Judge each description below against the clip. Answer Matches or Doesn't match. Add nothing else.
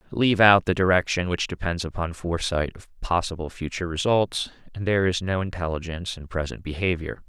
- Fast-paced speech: Doesn't match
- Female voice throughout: Doesn't match